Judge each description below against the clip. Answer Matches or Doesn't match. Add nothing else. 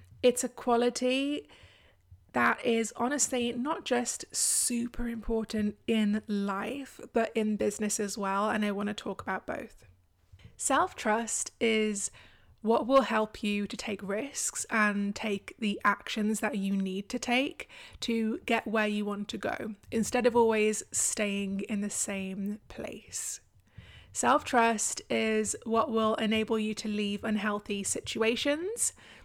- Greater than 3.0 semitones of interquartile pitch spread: Doesn't match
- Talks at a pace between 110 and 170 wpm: Matches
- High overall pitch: Matches